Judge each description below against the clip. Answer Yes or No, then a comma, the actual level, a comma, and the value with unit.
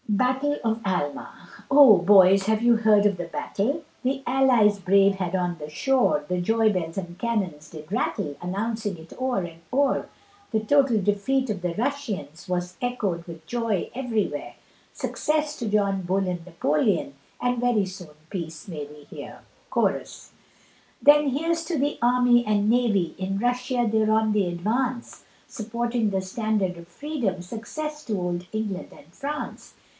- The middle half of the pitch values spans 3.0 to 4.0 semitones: No, average, 5.3 semitones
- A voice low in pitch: No, high, 210 Hz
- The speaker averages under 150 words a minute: No, average, 155 wpm